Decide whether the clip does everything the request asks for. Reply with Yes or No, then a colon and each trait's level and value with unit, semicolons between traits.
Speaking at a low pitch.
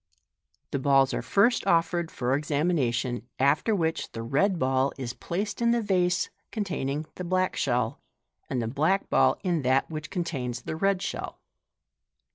No: medium, 155 Hz